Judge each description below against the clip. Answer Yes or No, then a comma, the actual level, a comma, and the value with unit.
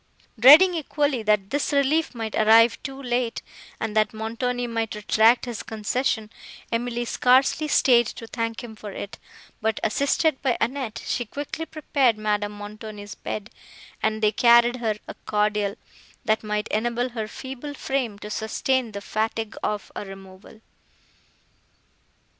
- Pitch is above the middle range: Yes, high, 230 Hz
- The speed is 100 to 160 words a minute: Yes, average, 140 wpm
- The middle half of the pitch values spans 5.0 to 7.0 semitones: No, average, 3.1 semitones